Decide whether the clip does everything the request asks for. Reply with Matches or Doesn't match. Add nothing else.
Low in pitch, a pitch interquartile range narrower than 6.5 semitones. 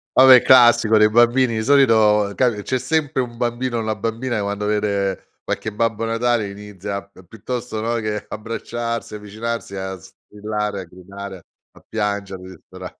Matches